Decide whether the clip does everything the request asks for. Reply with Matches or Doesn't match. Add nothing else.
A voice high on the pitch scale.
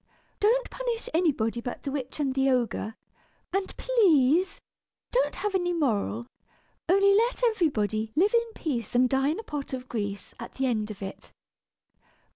Matches